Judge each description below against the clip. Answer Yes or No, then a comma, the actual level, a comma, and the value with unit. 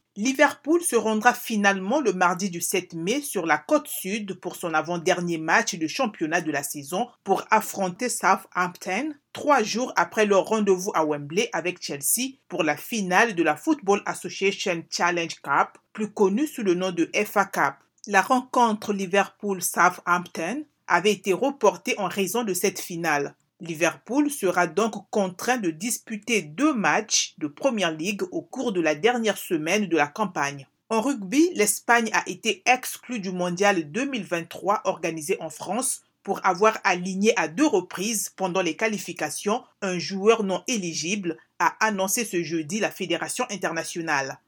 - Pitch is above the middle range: Yes, high, 195 Hz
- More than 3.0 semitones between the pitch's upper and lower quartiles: Yes, average, 4.6 semitones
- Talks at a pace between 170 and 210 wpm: No, average, 155 wpm